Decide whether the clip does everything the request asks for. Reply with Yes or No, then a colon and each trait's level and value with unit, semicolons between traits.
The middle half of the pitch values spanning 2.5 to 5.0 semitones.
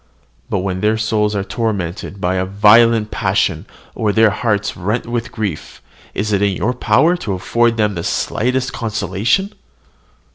Yes: average, 3.0 semitones